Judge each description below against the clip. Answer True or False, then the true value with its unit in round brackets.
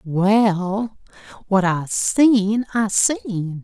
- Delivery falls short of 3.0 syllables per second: True (2.4 syllables/s)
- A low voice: False (205 Hz)